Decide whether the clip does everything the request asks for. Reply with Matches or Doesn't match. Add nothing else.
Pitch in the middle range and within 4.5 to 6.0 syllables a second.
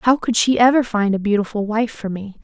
Doesn't match